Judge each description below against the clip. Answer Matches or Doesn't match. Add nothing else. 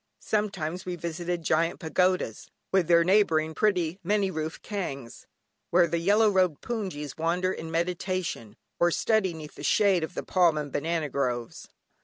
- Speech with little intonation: Doesn't match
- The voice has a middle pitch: Matches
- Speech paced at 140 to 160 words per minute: Matches